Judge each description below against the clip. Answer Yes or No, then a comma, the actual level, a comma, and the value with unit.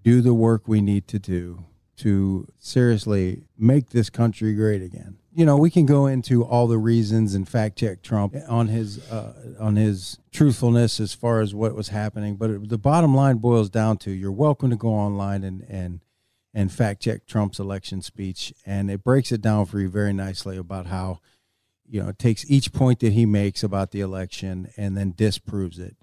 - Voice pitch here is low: Yes, low, 110 Hz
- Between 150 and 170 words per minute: No, average, 200 wpm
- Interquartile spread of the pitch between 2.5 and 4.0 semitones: Yes, average, 3.1 semitones